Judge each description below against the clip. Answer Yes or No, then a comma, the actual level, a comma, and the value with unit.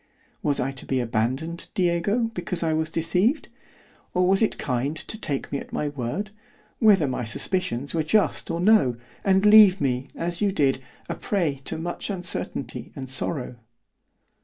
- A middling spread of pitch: No, wide, 6.0 semitones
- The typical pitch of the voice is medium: Yes, medium, 165 Hz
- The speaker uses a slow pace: No, average, 165 wpm